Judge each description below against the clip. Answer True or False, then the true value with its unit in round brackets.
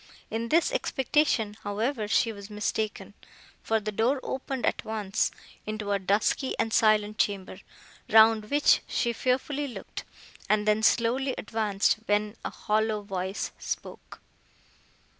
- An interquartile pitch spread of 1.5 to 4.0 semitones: True (2.4 semitones)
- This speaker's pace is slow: True (130 wpm)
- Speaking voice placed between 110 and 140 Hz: False (220 Hz)